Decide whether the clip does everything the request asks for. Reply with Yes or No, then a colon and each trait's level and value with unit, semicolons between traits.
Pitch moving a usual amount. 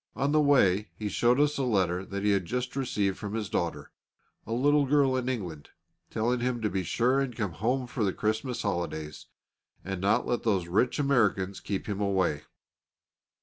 Yes: average, 4.9 semitones